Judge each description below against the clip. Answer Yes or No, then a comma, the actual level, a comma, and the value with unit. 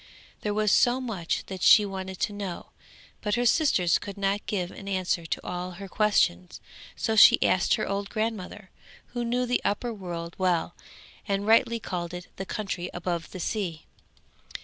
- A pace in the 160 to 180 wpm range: Yes, average, 170 wpm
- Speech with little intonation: No, average, 3.1 semitones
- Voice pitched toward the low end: No, high, 195 Hz